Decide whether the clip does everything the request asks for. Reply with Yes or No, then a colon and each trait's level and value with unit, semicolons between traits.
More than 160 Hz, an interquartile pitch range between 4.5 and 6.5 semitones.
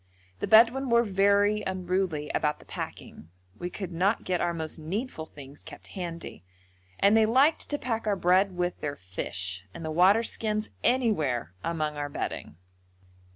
Yes: medium, 185 Hz; wide, 5.6 semitones